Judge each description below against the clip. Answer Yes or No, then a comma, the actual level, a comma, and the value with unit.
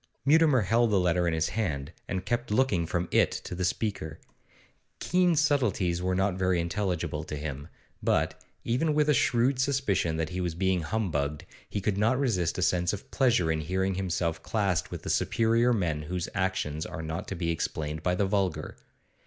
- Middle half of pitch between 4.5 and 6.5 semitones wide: Yes, average, 5.1 semitones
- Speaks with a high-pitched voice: No, very low, 95 Hz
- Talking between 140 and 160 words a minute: No, average, 185 wpm